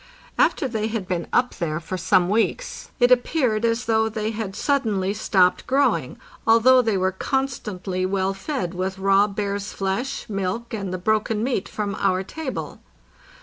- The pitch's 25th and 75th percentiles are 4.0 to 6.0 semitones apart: No, average, 3.6 semitones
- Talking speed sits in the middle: Yes, average, 165 wpm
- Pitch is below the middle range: No, high, 210 Hz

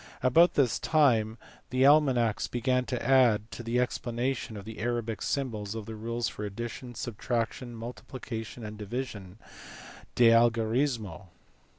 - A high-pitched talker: No, low, 120 Hz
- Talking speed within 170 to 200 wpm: No, slow, 135 wpm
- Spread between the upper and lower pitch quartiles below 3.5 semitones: Yes, narrow, 2.6 semitones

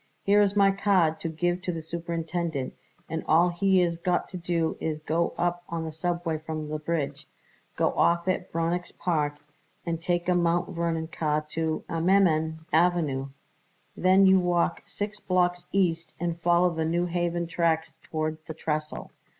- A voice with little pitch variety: Yes, narrow, 1.7 semitones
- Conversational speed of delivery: Yes, average, 170 wpm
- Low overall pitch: No, medium, 170 Hz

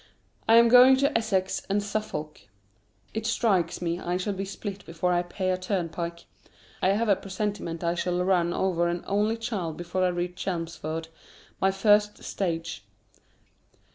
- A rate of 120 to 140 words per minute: No, average, 160 wpm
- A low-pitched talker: No, medium, 185 Hz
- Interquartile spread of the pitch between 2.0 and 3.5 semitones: Yes, average, 3.2 semitones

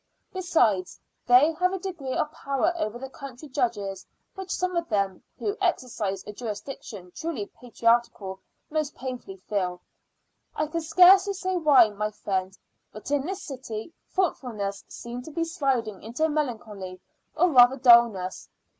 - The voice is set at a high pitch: Yes, very high, 250 Hz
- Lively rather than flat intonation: Yes, wide, 7.2 semitones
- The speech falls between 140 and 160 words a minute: Yes, average, 145 wpm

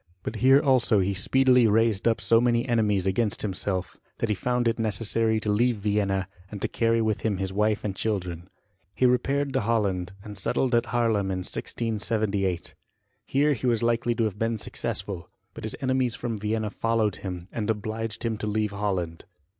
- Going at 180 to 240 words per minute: Yes, average, 185 wpm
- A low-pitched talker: Yes, low, 110 Hz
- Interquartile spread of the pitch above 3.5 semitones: No, average, 2.8 semitones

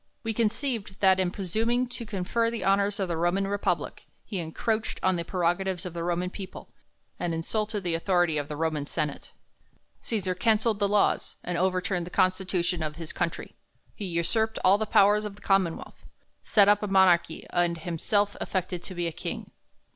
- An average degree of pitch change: Yes, average, 3.1 semitones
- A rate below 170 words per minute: No, average, 180 wpm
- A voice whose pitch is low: No, medium, 185 Hz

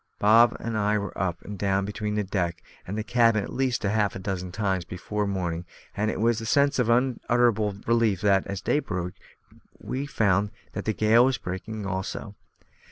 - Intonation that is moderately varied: Yes, average, 3.2 semitones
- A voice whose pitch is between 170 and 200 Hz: No, low, 105 Hz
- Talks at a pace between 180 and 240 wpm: Yes, average, 195 wpm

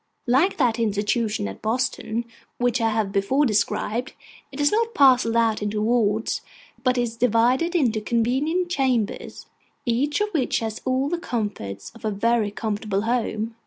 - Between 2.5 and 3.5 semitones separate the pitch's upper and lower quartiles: Yes, average, 3.2 semitones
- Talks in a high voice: Yes, high, 235 Hz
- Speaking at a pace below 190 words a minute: Yes, average, 155 wpm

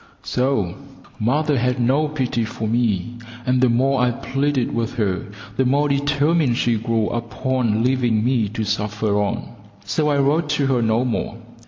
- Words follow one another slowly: No, average, 165 wpm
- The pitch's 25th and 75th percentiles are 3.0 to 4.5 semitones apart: Yes, average, 3.4 semitones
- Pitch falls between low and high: No, low, 125 Hz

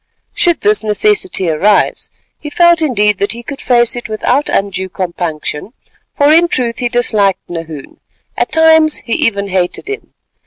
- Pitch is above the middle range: Yes, high, 230 Hz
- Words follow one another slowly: No, average, 155 wpm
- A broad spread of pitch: Yes, wide, 7.2 semitones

